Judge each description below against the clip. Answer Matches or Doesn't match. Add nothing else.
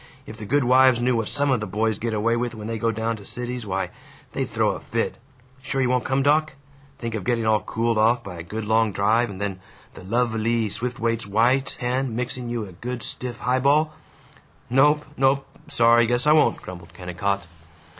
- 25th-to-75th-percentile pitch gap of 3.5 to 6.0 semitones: Doesn't match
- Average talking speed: Doesn't match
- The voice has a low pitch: Matches